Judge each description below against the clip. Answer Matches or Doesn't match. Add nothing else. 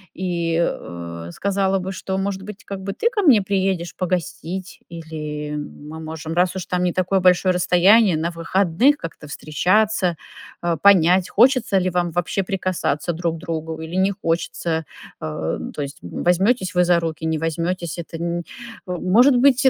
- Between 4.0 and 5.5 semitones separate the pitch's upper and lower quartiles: Doesn't match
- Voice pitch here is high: Doesn't match